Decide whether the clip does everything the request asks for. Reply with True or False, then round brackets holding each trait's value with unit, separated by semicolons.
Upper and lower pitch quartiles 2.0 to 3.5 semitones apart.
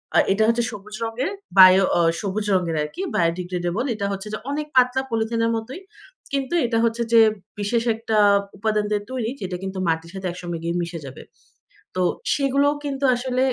False (5.0 semitones)